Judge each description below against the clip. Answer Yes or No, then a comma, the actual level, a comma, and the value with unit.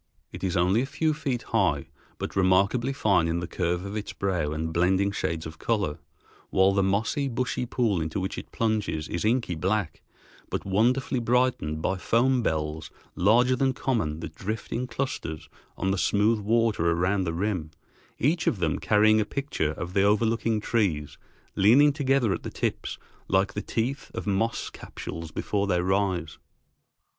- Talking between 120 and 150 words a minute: No, average, 170 wpm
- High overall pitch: No, low, 100 Hz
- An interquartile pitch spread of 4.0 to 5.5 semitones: Yes, average, 5.1 semitones